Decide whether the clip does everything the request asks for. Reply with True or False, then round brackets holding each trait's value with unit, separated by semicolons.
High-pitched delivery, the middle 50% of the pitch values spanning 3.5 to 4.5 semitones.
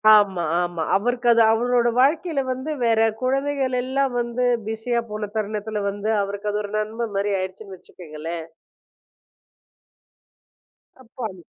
True (220 Hz; 3.9 semitones)